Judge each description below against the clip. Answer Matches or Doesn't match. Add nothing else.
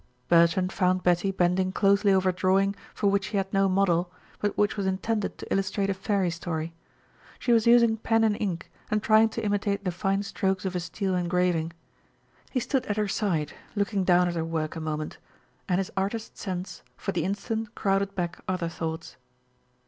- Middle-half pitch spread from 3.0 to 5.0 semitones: Doesn't match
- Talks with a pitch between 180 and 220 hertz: Matches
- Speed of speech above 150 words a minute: Matches